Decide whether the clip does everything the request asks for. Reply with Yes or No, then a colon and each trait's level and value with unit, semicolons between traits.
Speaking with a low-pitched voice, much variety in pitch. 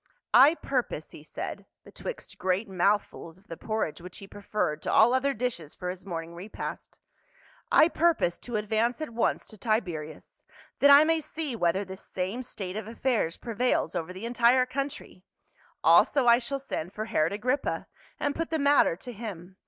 No: high, 220 Hz; wide, 6.0 semitones